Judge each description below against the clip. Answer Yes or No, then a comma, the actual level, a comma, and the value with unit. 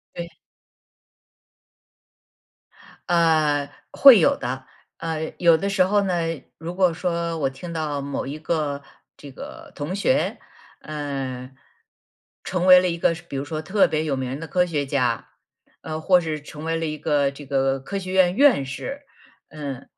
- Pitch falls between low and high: Yes, medium, 160 Hz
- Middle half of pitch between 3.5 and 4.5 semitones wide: Yes, average, 3.8 semitones